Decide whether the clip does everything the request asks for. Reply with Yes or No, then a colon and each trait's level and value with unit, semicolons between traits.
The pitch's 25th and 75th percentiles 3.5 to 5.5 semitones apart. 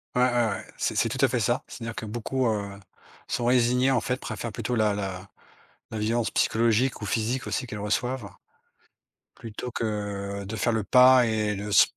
No: average, 2.9 semitones